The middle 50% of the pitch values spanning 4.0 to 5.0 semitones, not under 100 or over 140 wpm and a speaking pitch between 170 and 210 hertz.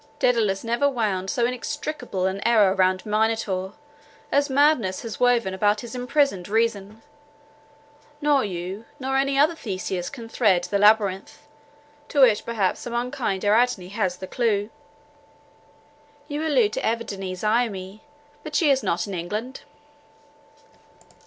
No: average, 4.5 semitones; slow, 135 wpm; high, 220 Hz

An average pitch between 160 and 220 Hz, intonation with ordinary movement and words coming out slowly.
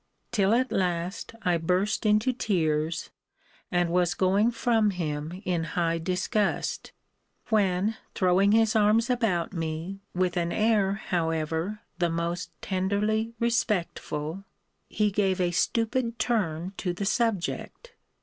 Yes: high, 190 Hz; average, 3.9 semitones; slow, 120 wpm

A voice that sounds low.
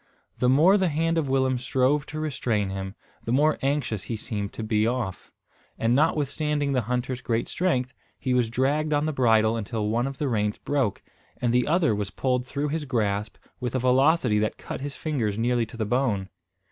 Yes: low, 125 Hz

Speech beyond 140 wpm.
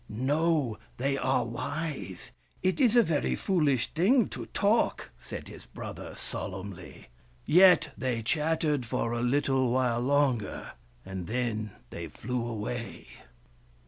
No: slow, 135 wpm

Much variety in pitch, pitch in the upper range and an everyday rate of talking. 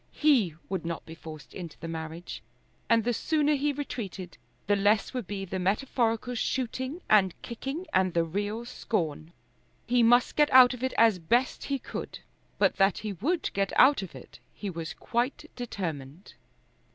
Yes: wide, 5.9 semitones; high, 215 Hz; average, 170 wpm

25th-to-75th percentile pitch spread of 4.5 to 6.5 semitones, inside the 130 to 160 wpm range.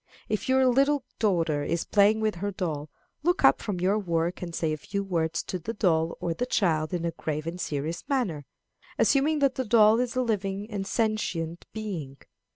No: average, 5.1 semitones; average, 195 wpm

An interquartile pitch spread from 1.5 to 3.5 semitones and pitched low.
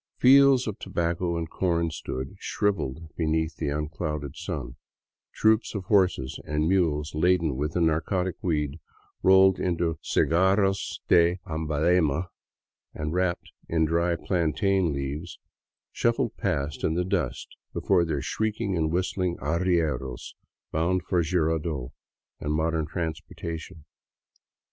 Yes: average, 3.0 semitones; very low, 85 Hz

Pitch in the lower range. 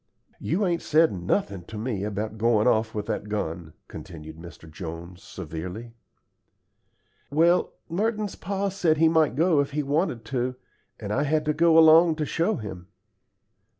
Yes: low, 125 Hz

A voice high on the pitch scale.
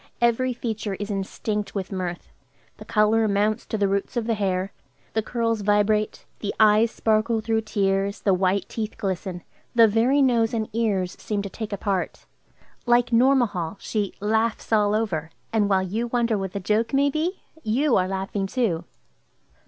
Yes: high, 215 Hz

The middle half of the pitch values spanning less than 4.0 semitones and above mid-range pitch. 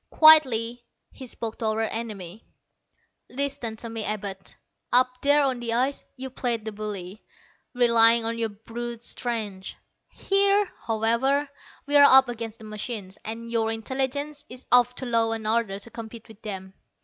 Yes: average, 2.7 semitones; high, 230 Hz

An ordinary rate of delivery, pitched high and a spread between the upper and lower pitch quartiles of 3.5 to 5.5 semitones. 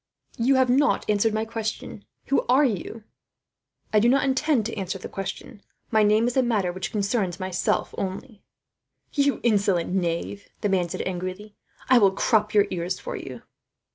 Yes: average, 175 wpm; high, 210 Hz; average, 4.0 semitones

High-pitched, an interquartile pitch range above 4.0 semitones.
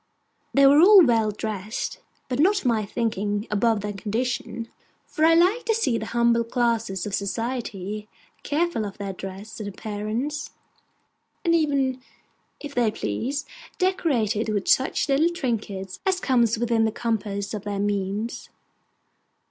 Yes: high, 230 Hz; average, 5.0 semitones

